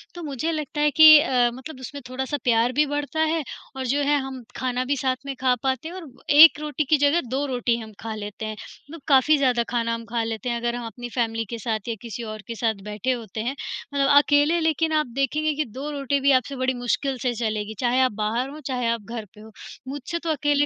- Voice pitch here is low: No, very high, 260 Hz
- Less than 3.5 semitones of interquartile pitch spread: No, average, 3.8 semitones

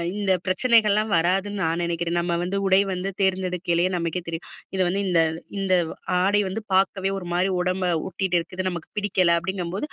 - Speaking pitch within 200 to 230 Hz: No, medium, 185 Hz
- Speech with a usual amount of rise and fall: No, narrow, 1.9 semitones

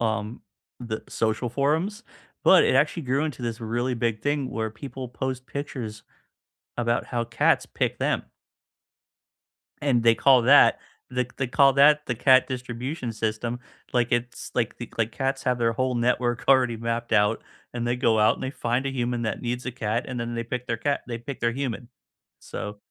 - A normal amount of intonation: No, narrow, 2.2 semitones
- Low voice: Yes, low, 120 Hz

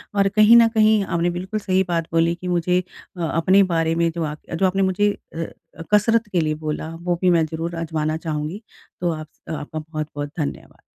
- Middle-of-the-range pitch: Yes, medium, 170 Hz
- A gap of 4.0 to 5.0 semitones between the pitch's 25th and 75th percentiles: No, average, 2.9 semitones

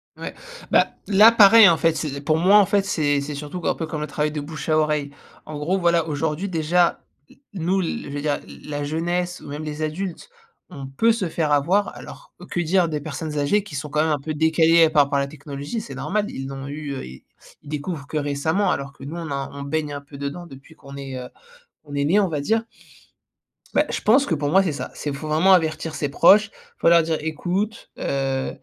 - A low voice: No, medium, 155 Hz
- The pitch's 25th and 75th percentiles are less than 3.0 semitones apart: No, average, 3.6 semitones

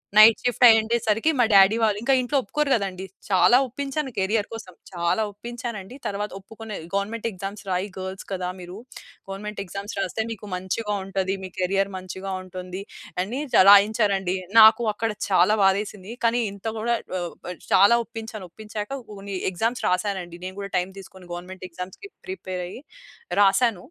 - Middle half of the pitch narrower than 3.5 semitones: Yes, average, 3.0 semitones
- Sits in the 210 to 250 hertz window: No, high, 200 Hz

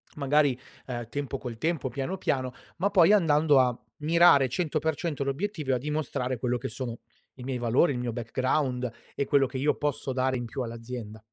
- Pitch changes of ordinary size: Yes, average, 3.4 semitones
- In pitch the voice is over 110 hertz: Yes, low, 135 Hz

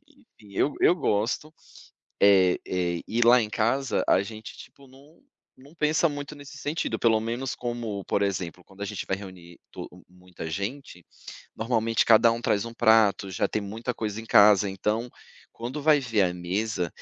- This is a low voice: Yes, low, 110 Hz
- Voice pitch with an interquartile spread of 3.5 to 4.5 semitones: Yes, average, 4.0 semitones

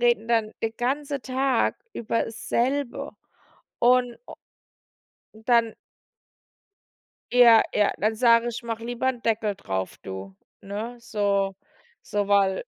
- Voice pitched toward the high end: Yes, high, 230 Hz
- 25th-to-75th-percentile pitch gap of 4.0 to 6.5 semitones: No, average, 2.7 semitones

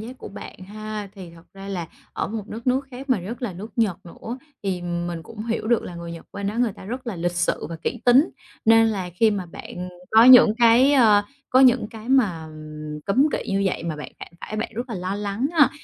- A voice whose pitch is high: Yes, high, 210 Hz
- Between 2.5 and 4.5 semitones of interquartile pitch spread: No, average, 5.0 semitones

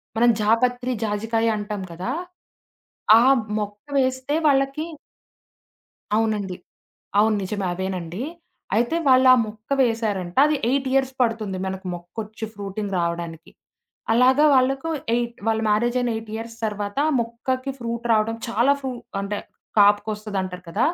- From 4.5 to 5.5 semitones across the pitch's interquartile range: No, average, 3.5 semitones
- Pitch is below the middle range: No, high, 220 Hz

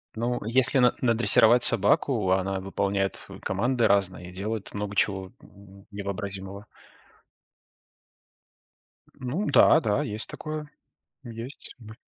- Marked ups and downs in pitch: No, average, 3.7 semitones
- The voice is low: Yes, low, 105 Hz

